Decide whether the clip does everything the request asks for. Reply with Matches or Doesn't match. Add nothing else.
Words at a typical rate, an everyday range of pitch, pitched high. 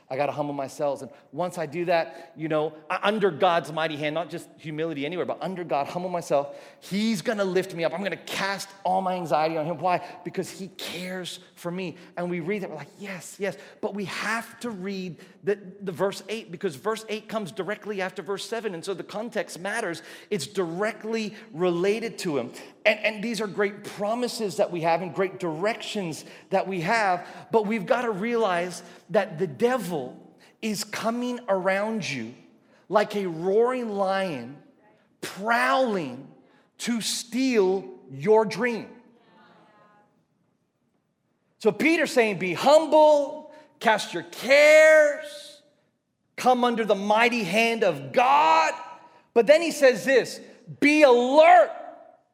Matches